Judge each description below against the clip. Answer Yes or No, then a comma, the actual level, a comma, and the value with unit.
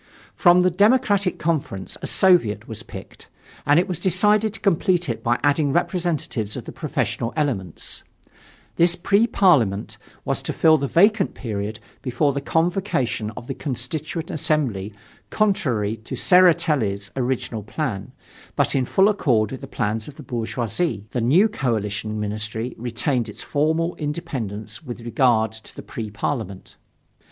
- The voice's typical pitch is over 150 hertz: No, low, 135 Hz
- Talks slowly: No, average, 145 wpm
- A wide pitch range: Yes, wide, 7.7 semitones